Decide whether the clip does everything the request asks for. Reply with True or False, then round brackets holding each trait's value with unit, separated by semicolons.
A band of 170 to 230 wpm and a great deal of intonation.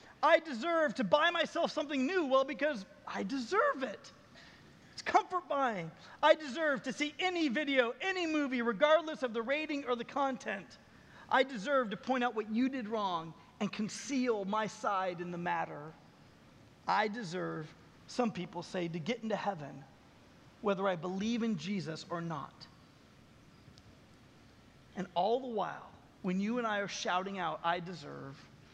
False (155 wpm; 7.1 semitones)